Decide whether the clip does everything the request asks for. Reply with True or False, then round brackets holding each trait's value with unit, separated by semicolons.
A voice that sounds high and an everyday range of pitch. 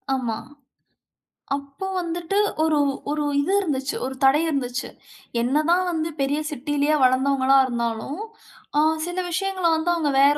True (290 Hz; 3.8 semitones)